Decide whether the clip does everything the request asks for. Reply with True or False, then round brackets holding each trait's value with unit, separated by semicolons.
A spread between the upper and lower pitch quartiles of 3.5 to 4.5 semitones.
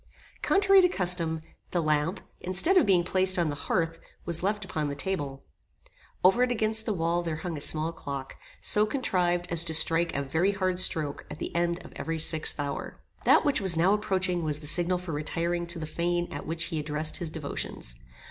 False (3.0 semitones)